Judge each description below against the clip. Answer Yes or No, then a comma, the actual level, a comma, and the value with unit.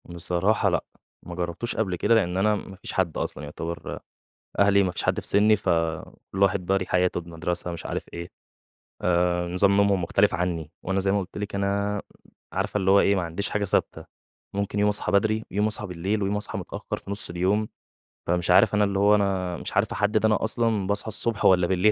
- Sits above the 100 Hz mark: No, very low, 95 Hz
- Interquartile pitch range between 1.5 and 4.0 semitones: Yes, average, 2.7 semitones